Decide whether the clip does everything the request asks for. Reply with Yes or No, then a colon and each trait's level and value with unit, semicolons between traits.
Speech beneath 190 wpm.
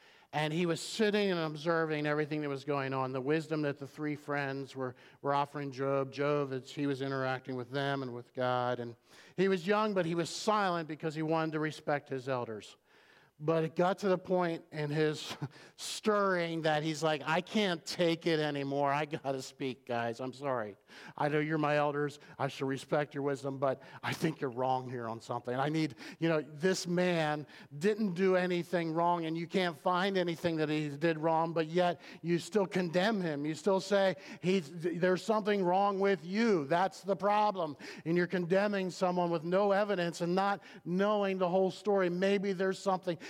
No: average, 195 wpm